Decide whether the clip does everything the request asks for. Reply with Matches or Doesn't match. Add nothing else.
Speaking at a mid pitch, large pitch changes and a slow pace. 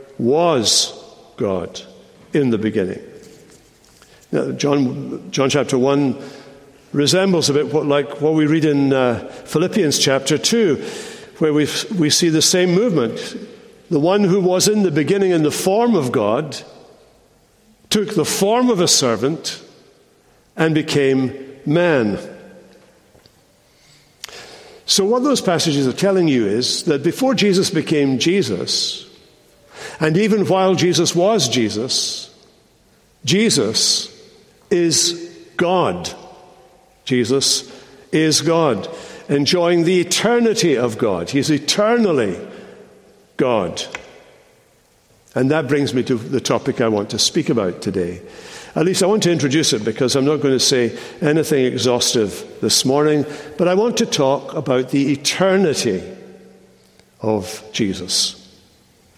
Matches